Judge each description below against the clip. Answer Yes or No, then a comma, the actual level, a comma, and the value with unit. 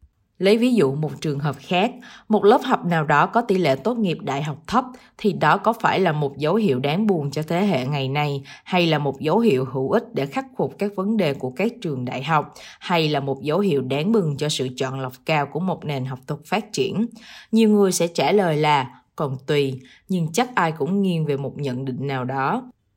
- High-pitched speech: No, medium, 155 Hz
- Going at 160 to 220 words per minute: No, average, 240 wpm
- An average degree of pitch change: No, wide, 6.8 semitones